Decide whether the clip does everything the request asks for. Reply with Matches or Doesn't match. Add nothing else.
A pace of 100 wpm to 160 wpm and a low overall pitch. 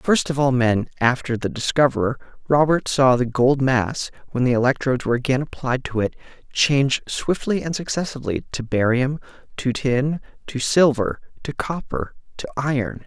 Matches